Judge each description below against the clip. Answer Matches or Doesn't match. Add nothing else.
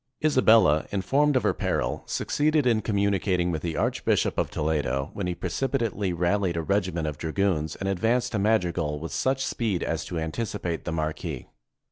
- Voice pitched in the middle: Doesn't match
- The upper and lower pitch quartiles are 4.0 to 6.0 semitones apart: Matches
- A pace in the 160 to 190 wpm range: Matches